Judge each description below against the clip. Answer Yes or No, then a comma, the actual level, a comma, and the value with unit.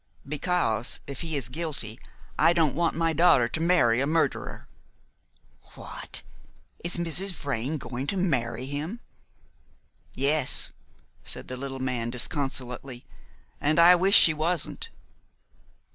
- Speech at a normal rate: No, slow, 125 wpm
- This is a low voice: No, medium, 145 Hz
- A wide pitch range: No, average, 4.8 semitones